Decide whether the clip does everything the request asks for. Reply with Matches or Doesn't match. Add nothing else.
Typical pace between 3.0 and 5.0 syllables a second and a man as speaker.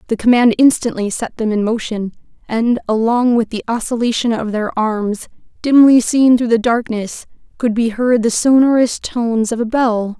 Doesn't match